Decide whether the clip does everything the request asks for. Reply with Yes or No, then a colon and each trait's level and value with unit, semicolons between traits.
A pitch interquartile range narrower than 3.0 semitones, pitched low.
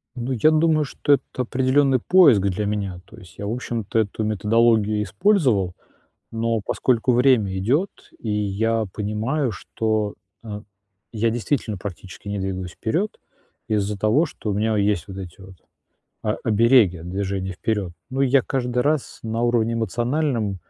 No: average, 3.8 semitones; low, 110 Hz